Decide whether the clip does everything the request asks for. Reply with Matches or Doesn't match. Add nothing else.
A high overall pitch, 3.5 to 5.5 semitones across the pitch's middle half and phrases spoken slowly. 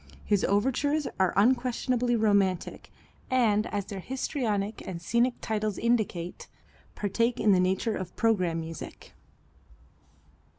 Matches